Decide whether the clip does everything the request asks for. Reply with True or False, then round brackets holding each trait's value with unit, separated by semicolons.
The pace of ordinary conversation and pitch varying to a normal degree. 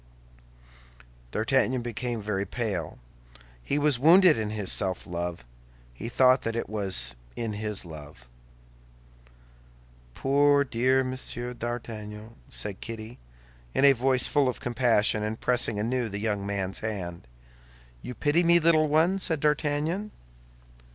False (130 wpm; 4.6 semitones)